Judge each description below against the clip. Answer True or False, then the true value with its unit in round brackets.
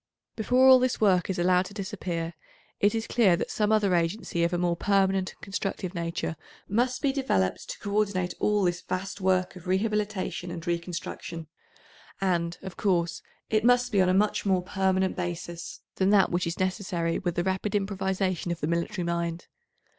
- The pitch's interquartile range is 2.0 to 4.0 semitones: True (2.9 semitones)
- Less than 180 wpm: False (185 wpm)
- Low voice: False (185 Hz)